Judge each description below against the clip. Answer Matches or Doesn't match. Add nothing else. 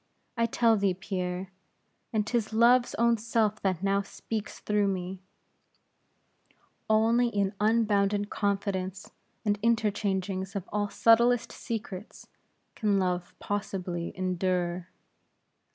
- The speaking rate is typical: Doesn't match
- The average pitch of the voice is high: Matches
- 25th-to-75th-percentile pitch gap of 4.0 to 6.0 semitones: Doesn't match